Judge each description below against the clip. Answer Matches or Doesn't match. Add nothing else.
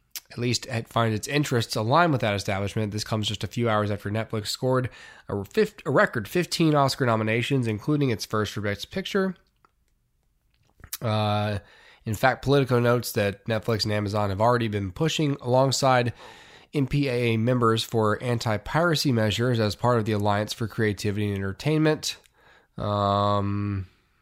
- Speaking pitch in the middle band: Doesn't match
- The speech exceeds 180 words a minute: Doesn't match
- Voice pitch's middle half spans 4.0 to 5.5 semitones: Doesn't match